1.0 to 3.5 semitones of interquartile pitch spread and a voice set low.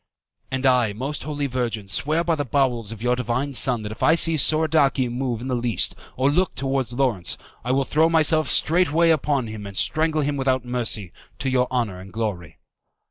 No: average, 3.9 semitones; low, 130 Hz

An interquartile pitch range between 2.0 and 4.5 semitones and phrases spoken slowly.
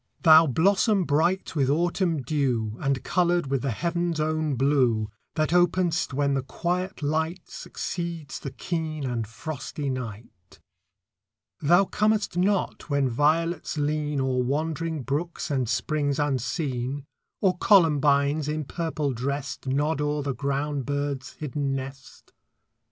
Yes: average, 3.6 semitones; slow, 130 wpm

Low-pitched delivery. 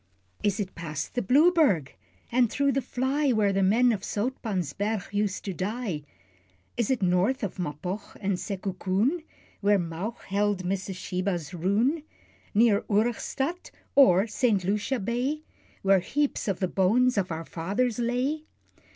No: high, 205 Hz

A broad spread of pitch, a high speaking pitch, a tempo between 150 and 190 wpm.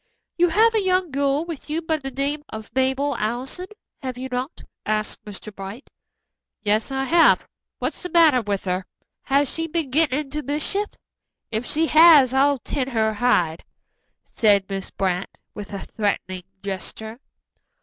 Yes: wide, 6.2 semitones; very high, 265 Hz; average, 160 wpm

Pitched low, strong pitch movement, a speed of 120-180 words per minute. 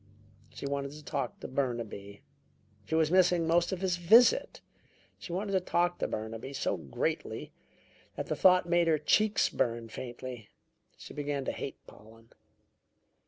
No: medium, 145 Hz; wide, 6.7 semitones; average, 155 wpm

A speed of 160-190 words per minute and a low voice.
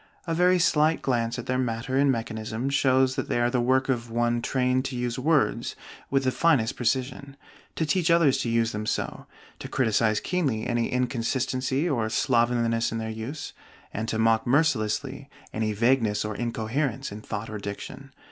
Yes: average, 175 wpm; low, 125 Hz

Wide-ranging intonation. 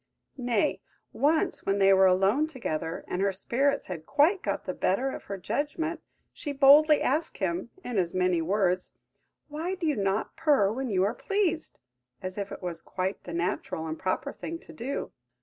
Yes: wide, 7.9 semitones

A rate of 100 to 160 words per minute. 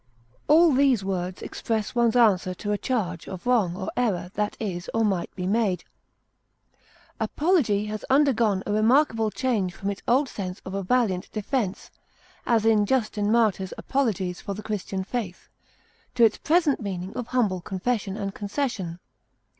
Yes: average, 155 wpm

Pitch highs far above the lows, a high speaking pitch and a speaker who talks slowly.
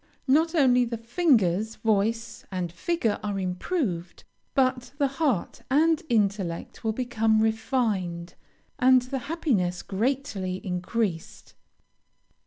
Yes: wide, 5.7 semitones; high, 225 Hz; slow, 105 wpm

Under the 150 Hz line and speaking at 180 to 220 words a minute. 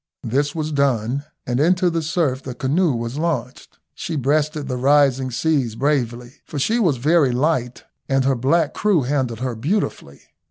No: medium, 140 Hz; average, 165 wpm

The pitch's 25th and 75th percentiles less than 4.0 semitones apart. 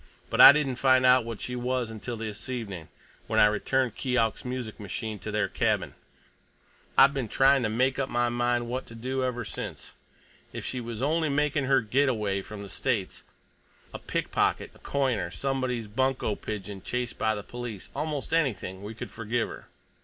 Yes: average, 3.3 semitones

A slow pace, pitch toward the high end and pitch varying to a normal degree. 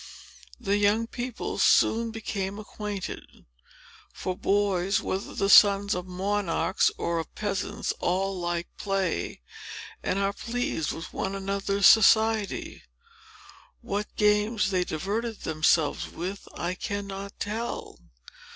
No: slow, 115 wpm; high, 200 Hz; narrow, 2.2 semitones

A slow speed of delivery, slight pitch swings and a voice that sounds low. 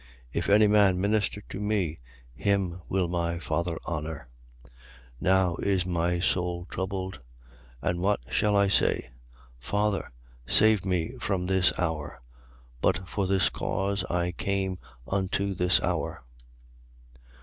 Yes: slow, 125 wpm; narrow, 2.2 semitones; very low, 95 Hz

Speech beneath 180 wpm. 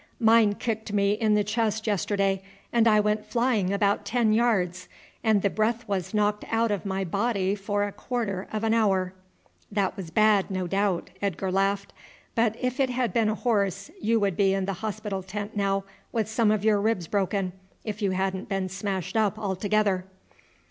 No: average, 185 wpm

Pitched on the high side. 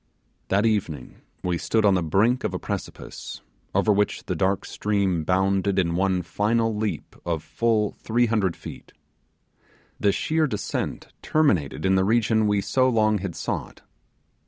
No: low, 100 Hz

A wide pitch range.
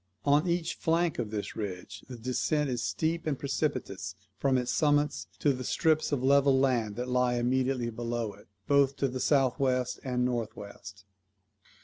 No: average, 3.1 semitones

